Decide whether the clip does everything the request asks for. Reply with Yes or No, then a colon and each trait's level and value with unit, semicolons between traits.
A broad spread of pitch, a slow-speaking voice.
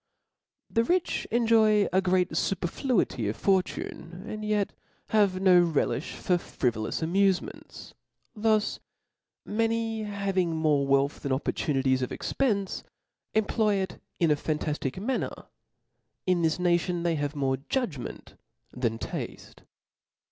Yes: wide, 5.9 semitones; slow, 120 wpm